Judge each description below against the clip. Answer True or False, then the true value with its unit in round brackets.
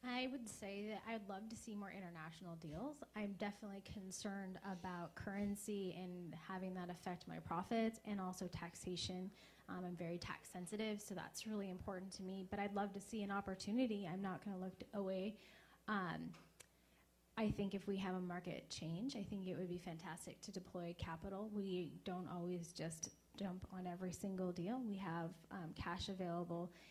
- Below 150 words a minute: False (180 wpm)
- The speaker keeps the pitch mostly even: True (2.3 semitones)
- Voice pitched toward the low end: False (190 Hz)